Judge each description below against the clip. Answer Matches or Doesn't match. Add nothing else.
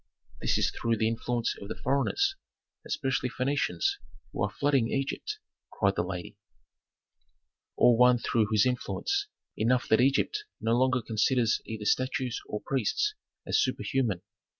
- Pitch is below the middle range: Matches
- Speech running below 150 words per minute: Matches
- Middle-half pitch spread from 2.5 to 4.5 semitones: Matches